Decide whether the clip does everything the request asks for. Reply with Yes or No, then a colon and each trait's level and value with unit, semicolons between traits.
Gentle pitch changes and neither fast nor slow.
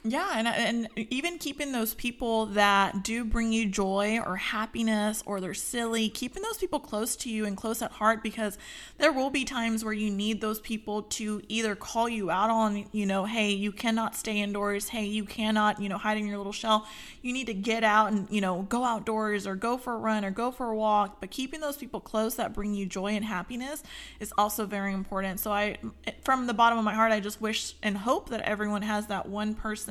No: narrow, 1.8 semitones; fast, 230 wpm